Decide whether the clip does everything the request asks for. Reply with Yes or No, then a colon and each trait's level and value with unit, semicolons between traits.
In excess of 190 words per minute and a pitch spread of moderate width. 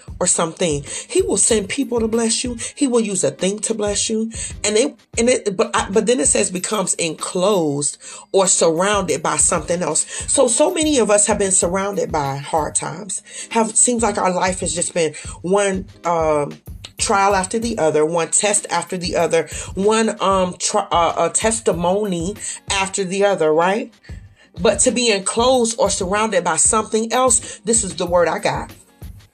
No: average, 185 wpm; average, 4.5 semitones